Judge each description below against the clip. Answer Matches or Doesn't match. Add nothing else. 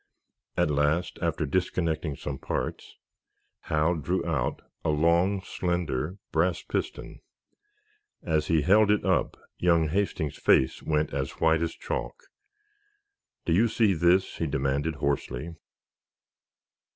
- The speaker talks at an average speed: Doesn't match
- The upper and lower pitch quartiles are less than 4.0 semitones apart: Matches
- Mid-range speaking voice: Doesn't match